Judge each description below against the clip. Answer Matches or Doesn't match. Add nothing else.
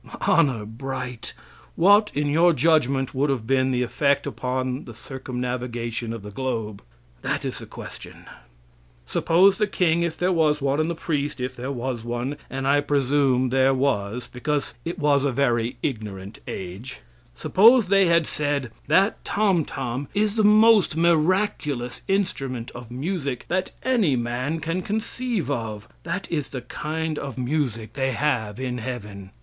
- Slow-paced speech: Doesn't match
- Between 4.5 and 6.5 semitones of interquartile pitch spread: Matches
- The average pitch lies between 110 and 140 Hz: Matches